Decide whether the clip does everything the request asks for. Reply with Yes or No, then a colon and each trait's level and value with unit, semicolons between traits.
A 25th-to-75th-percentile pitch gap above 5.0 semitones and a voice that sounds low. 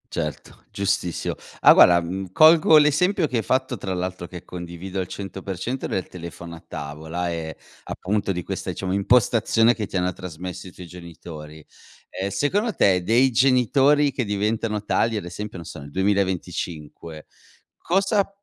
Yes: wide, 5.4 semitones; very low, 95 Hz